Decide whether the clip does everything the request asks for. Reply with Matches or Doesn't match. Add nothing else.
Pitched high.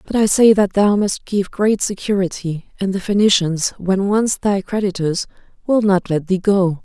Matches